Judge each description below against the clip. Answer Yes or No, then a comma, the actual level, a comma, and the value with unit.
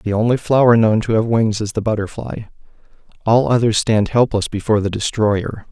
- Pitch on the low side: Yes, low, 110 Hz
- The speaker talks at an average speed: Yes, average, 180 wpm